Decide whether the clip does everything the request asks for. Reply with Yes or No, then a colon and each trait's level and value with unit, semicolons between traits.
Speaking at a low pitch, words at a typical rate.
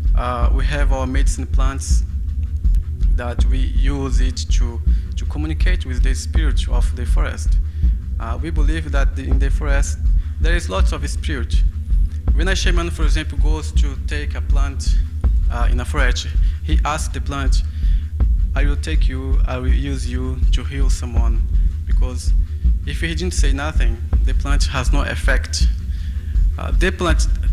Yes: very low, 75 Hz; average, 160 wpm